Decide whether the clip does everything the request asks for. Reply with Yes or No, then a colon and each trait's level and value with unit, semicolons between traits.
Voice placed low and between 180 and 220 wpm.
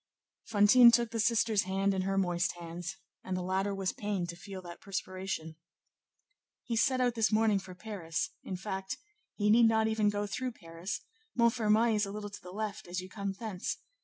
No: high, 200 Hz; average, 190 wpm